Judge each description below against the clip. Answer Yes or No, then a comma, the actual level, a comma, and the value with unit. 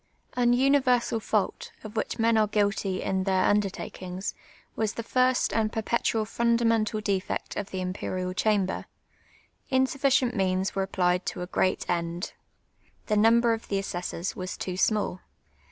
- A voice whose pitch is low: No, high, 210 Hz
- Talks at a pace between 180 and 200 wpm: No, average, 150 wpm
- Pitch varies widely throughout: No, average, 3.7 semitones